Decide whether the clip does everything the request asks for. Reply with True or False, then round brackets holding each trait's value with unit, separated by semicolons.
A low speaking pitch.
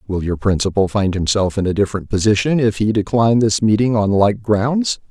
True (105 Hz)